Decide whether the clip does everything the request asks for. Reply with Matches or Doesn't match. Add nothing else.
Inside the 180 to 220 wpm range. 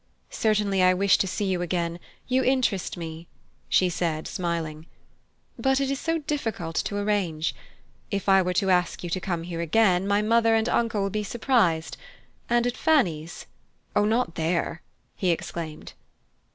Doesn't match